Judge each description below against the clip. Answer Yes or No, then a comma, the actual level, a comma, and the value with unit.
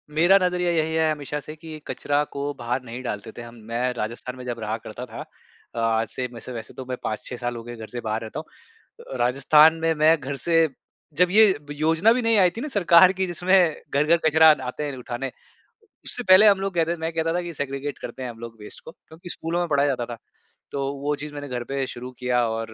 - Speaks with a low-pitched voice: No, medium, 145 Hz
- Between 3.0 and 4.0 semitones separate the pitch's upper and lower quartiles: No, average, 5.1 semitones